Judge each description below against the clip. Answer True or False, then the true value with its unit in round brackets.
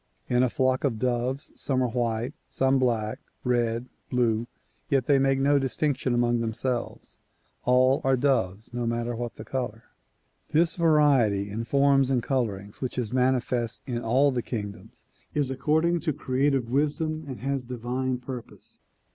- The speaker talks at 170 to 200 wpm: False (155 wpm)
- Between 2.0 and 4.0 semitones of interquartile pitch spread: True (2.5 semitones)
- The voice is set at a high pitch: False (125 Hz)